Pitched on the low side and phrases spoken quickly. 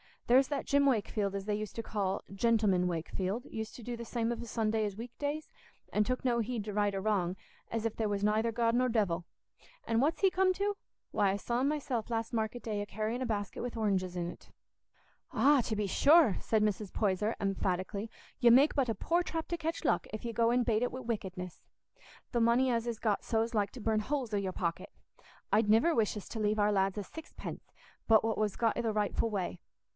No: high, 220 Hz; fast, 230 wpm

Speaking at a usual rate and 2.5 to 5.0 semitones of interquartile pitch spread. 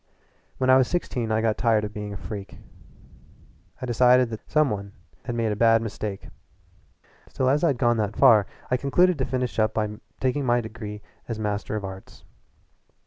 Yes: average, 190 wpm; average, 3.3 semitones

